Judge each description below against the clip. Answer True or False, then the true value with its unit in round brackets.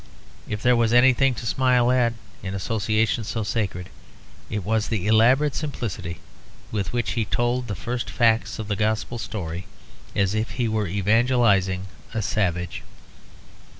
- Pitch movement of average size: True (3.3 semitones)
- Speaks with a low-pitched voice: True (110 Hz)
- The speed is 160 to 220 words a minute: False (150 wpm)